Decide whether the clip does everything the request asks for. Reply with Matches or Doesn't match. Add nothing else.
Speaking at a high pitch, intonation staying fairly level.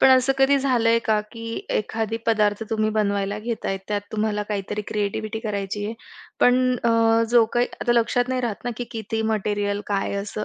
Matches